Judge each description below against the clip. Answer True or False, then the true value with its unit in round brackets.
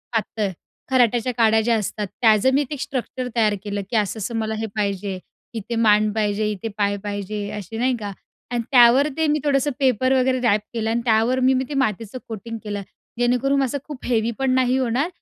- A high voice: True (230 Hz)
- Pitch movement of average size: True (3.4 semitones)